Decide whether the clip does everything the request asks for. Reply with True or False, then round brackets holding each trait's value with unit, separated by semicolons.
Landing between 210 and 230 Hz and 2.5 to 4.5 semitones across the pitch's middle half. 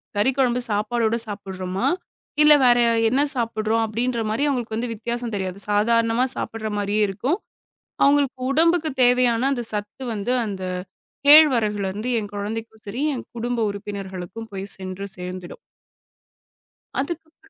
True (225 Hz; 3.5 semitones)